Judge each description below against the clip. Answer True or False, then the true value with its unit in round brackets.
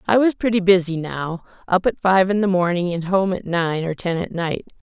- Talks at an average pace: False (230 wpm)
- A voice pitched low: False (185 Hz)